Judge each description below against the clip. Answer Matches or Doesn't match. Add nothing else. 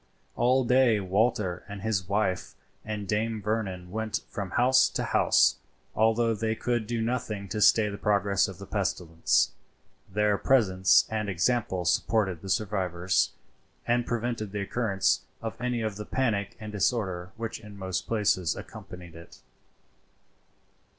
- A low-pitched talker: Matches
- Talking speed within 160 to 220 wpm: Doesn't match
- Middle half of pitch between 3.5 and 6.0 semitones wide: Doesn't match